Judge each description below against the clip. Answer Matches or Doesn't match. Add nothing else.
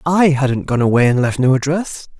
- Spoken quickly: Matches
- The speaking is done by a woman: Doesn't match